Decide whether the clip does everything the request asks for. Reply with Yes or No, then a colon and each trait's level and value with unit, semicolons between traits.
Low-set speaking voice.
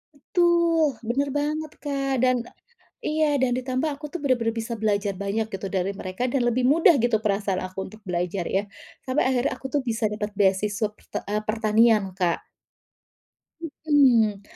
No: high, 230 Hz